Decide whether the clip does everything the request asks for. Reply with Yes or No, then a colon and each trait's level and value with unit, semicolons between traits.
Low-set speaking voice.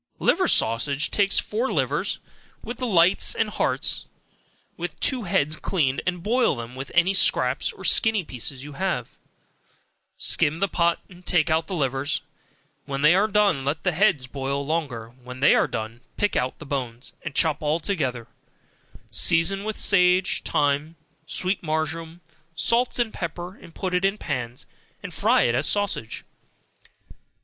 No: medium, 160 Hz